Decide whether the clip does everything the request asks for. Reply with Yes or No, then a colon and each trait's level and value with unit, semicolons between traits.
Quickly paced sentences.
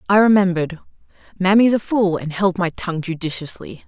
No: average, 155 wpm